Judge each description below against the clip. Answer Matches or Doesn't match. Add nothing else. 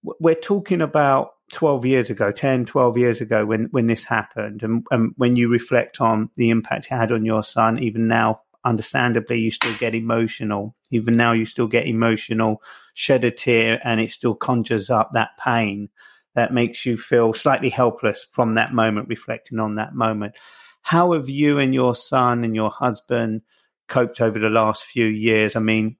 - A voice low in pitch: Matches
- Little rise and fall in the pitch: Matches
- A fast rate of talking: Doesn't match